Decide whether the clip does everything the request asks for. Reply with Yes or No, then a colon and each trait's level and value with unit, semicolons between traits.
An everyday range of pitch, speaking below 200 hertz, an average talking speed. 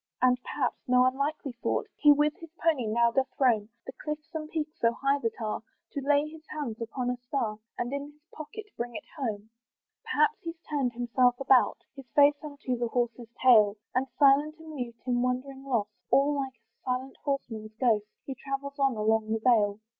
No: average, 3.3 semitones; very high, 260 Hz; average, 190 wpm